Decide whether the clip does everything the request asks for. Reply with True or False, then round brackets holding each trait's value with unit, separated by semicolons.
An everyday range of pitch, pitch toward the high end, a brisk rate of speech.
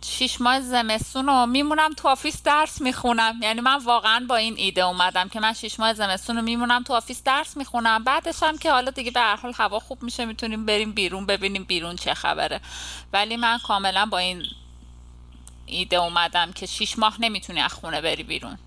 True (4.7 semitones; 225 Hz; 190 wpm)